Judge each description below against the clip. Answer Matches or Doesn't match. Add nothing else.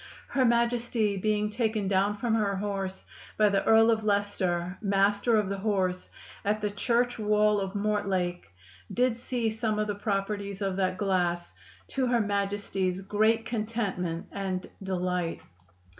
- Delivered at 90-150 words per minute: Matches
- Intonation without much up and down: Matches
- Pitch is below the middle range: Doesn't match